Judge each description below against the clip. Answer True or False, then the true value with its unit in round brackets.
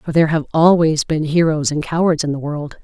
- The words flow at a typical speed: False (235 wpm)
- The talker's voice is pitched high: False (155 Hz)